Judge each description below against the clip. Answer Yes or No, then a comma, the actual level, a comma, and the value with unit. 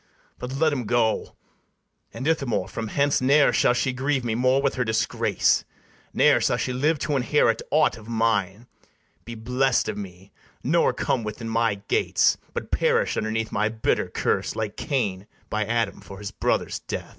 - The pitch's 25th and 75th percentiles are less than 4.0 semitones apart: Yes, average, 3.3 semitones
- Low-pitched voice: Yes, low, 115 Hz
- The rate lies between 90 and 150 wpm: No, average, 170 wpm